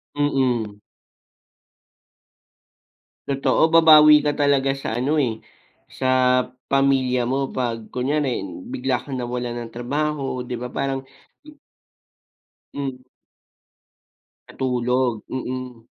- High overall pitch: No, low, 130 Hz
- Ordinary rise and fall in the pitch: No, narrow, 2.1 semitones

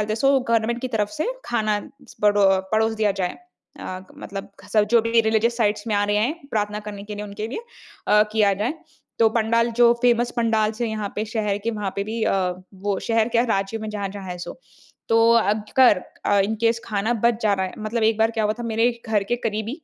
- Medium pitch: No, high, 220 Hz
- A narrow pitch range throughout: Yes, narrow, 2.0 semitones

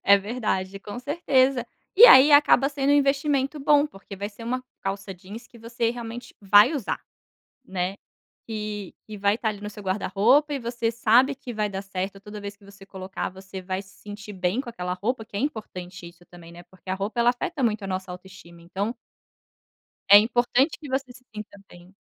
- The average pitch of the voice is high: Yes, high, 210 Hz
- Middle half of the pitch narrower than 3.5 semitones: No, average, 4.6 semitones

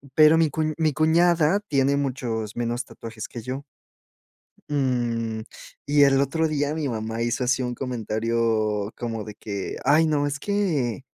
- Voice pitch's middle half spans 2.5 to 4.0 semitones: No, average, 4.6 semitones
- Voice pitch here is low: Yes, low, 130 Hz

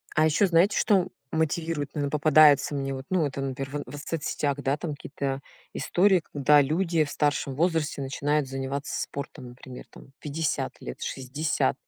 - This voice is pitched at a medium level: Yes, medium, 145 Hz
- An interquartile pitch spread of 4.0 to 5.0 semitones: No, average, 2.7 semitones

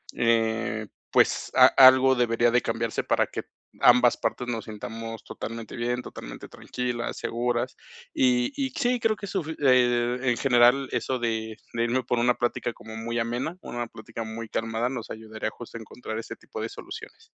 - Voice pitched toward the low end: Yes, low, 120 Hz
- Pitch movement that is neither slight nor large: No, narrow, 1.6 semitones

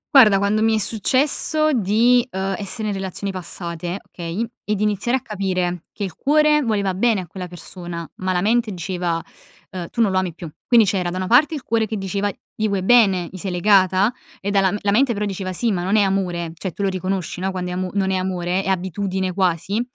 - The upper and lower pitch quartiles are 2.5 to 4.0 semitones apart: Yes, average, 2.8 semitones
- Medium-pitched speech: No, high, 195 Hz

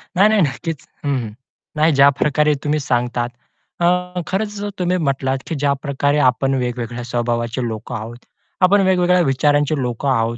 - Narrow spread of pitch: No, average, 4.7 semitones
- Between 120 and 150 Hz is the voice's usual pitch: Yes, medium, 140 Hz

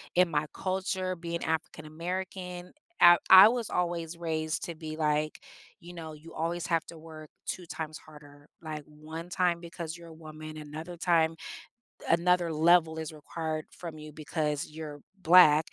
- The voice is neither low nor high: Yes, medium, 160 Hz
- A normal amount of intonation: No, narrow, 2.0 semitones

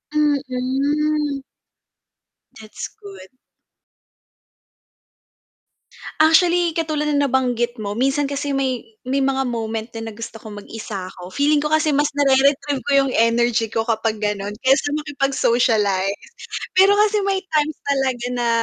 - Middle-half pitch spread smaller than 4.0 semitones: No, average, 4.6 semitones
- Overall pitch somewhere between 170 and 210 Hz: No, very high, 270 Hz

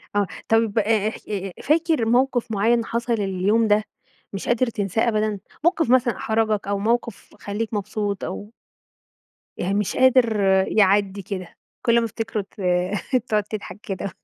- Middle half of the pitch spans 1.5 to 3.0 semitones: Yes, narrow, 2.5 semitones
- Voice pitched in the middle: No, high, 215 Hz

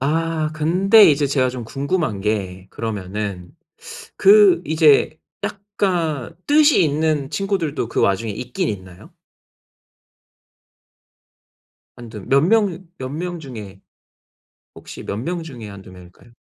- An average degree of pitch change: No, wide, 7.9 semitones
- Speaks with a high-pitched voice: No, medium, 145 Hz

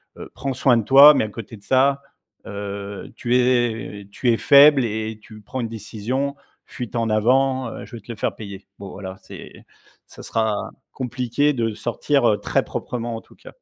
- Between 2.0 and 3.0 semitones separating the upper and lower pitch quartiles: No, average, 3.5 semitones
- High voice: No, low, 115 Hz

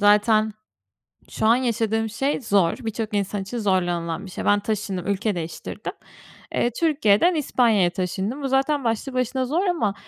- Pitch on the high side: Yes, high, 220 Hz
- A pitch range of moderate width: Yes, average, 4.3 semitones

